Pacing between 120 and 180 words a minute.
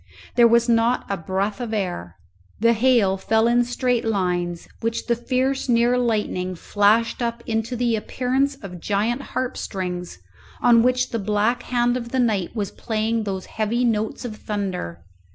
Yes: average, 165 wpm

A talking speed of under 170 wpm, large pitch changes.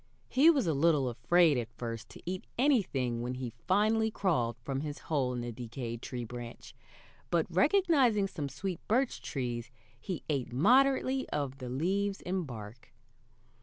Yes: average, 160 wpm; wide, 8.5 semitones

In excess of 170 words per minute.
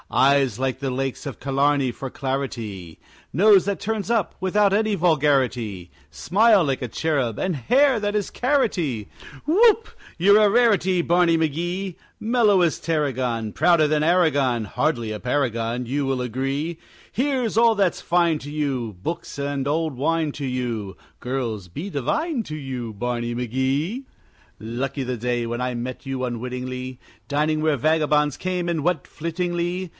No: average, 150 wpm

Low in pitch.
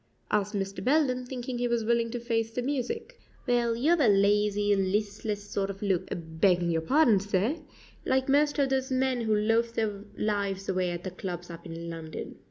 No: high, 210 Hz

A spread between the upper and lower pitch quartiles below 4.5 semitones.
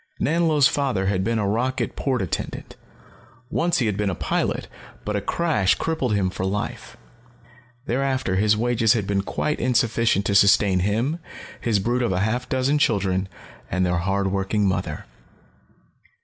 No: average, 4.8 semitones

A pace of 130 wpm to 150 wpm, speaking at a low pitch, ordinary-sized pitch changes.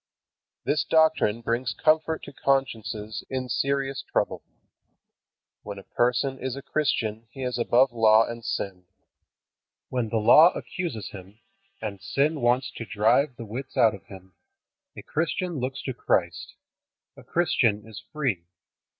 Yes: average, 140 wpm; low, 120 Hz; average, 4.3 semitones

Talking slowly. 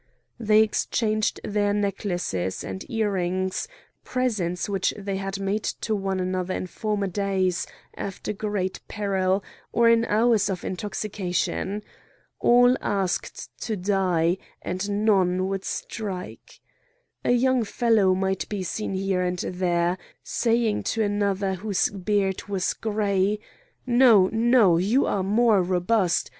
Yes: slow, 125 wpm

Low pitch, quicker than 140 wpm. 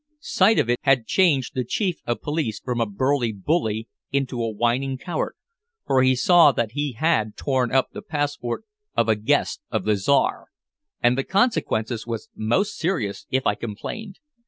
Yes: low, 130 Hz; average, 175 wpm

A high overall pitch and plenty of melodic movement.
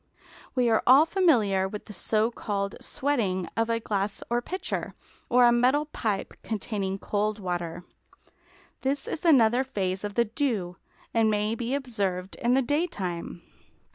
No: high, 220 Hz; average, 4.4 semitones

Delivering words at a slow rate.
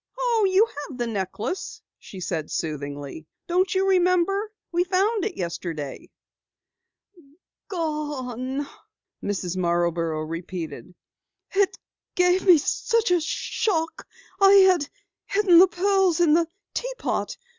Yes: slow, 115 wpm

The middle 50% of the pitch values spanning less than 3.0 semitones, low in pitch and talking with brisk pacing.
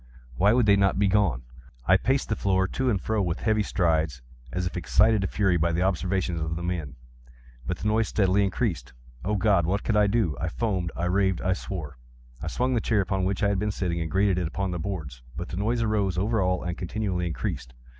No: average, 3.3 semitones; very low, 95 Hz; fast, 220 wpm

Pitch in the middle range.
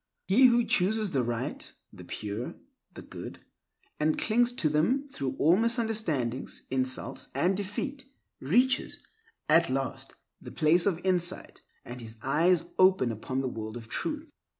Yes: medium, 170 Hz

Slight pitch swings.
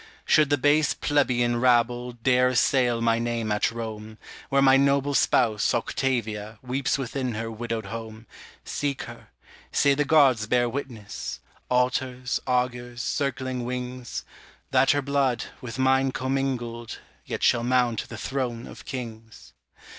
Yes: narrow, 2.3 semitones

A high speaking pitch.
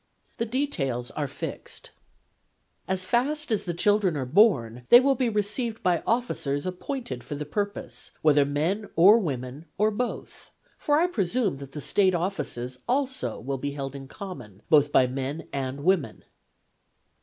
No: medium, 175 Hz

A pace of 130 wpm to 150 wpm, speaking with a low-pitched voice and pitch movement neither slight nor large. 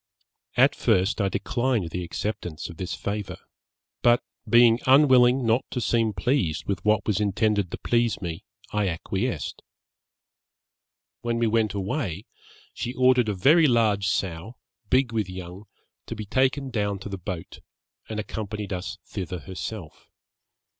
Yes: average, 145 wpm; low, 105 Hz; average, 4.2 semitones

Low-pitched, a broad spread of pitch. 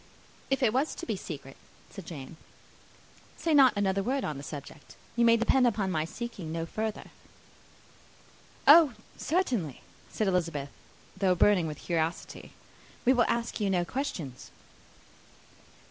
No: high, 195 Hz; wide, 6.6 semitones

